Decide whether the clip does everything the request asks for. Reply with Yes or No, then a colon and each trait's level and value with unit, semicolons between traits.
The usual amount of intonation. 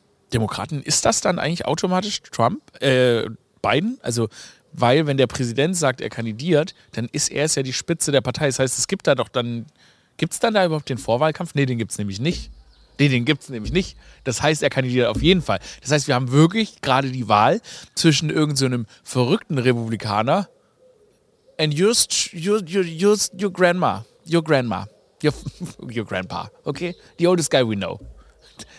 No: wide, 6.0 semitones